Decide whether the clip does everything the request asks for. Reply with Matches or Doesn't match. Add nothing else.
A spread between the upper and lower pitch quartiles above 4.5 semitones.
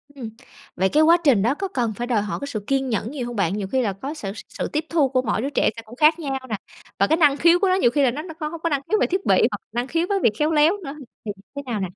Matches